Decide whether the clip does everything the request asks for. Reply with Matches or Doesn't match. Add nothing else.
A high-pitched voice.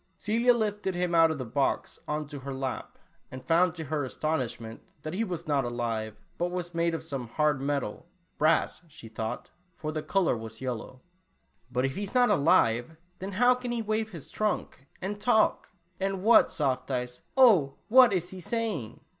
Doesn't match